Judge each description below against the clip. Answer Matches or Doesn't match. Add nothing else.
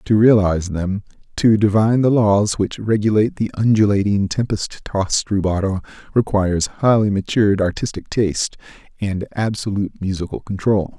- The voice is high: Doesn't match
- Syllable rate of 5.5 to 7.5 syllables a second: Doesn't match